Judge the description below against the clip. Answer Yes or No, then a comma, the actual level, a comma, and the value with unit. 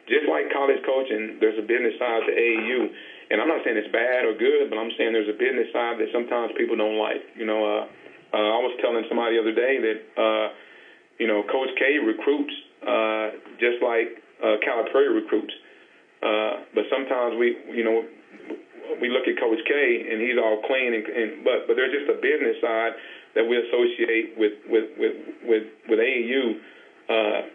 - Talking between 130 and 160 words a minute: No, average, 190 wpm